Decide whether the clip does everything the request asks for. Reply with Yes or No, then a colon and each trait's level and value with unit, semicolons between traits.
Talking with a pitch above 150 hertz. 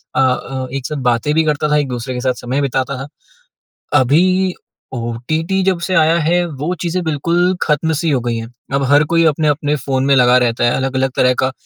No: medium, 140 Hz